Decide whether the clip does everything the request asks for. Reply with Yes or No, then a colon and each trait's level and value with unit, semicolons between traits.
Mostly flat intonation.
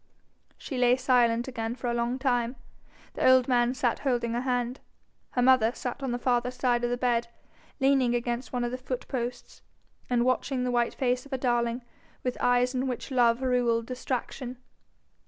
Yes: narrow, 1.1 semitones